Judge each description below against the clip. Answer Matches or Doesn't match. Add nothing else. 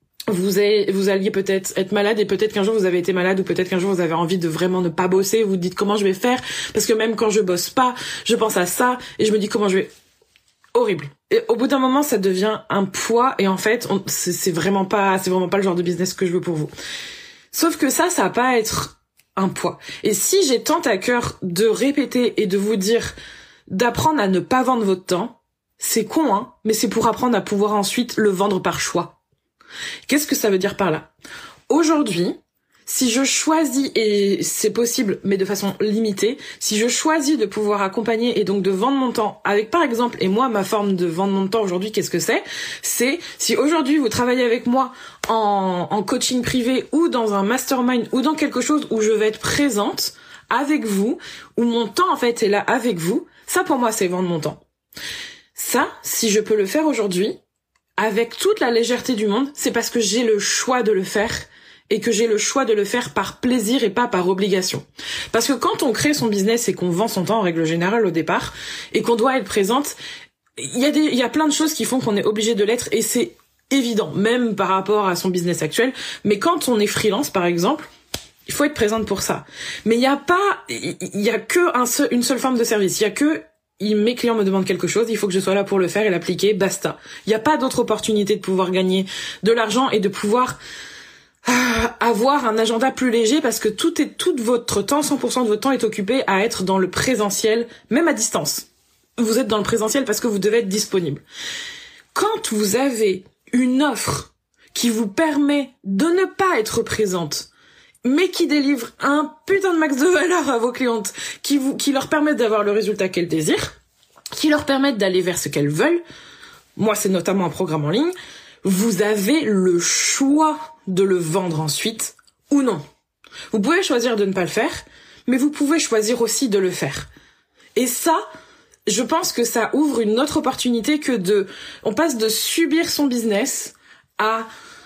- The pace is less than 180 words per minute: Doesn't match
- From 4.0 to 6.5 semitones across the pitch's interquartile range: Matches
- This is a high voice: Matches